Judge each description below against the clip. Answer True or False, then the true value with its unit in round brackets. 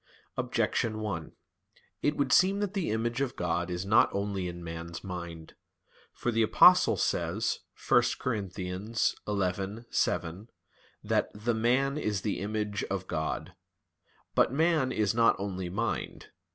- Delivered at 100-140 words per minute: True (135 wpm)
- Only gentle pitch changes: False (4.5 semitones)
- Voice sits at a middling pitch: False (105 Hz)